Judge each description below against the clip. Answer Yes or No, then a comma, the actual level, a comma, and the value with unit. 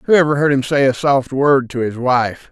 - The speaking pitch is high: No, low, 135 Hz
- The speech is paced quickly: Yes, fast, 265 wpm